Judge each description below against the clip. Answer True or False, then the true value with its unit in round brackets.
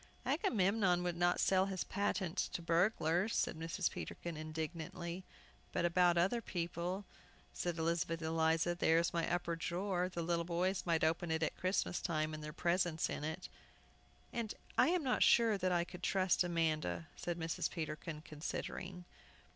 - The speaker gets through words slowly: False (160 wpm)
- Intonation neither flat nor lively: False (2.1 semitones)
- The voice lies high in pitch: False (175 Hz)